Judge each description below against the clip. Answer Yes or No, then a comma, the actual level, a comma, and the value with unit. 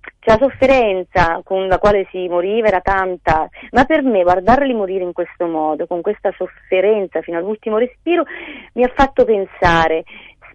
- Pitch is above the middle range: Yes, high, 195 Hz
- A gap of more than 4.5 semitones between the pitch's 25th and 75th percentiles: Yes, wide, 5.4 semitones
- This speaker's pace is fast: No, average, 160 wpm